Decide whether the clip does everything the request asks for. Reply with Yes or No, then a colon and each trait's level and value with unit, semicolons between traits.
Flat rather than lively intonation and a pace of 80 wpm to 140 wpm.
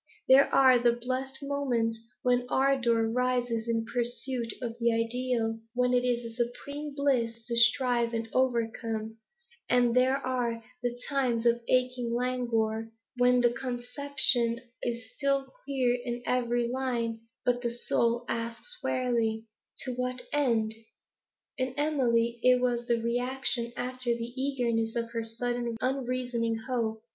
Yes: narrow, 1.6 semitones; slow, 135 wpm